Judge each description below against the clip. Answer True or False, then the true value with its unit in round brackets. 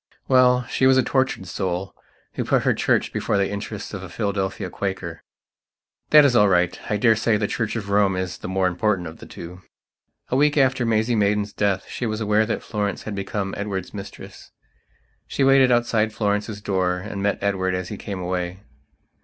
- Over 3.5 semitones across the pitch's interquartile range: False (3.0 semitones)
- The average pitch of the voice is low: True (100 Hz)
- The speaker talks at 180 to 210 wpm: True (185 wpm)